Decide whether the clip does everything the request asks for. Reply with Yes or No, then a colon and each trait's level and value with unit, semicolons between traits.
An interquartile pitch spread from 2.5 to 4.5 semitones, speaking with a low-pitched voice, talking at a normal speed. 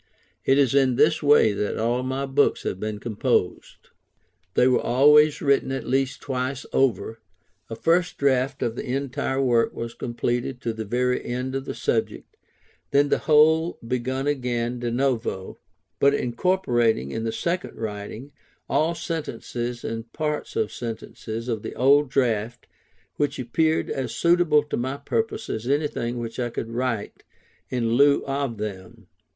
Yes: average, 3.4 semitones; low, 125 Hz; average, 155 wpm